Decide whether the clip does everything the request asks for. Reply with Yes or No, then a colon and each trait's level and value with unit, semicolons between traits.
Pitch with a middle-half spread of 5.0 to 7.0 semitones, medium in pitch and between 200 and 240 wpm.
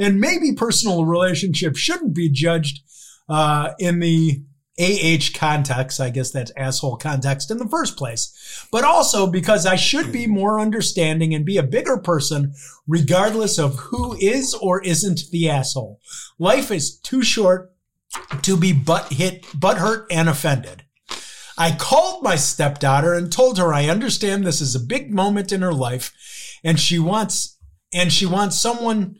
No: average, 5.3 semitones; medium, 170 Hz; average, 155 wpm